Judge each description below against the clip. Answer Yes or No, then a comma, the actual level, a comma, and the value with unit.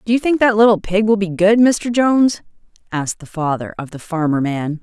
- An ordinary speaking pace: No, fast, 225 wpm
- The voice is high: Yes, high, 195 Hz